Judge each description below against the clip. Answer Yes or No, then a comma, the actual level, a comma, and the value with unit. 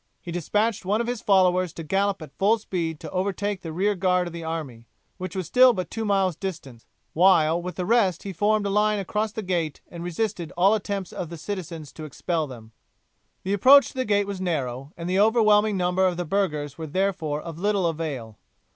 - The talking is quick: Yes, fast, 215 wpm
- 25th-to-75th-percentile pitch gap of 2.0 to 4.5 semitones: Yes, average, 3.8 semitones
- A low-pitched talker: No, medium, 185 Hz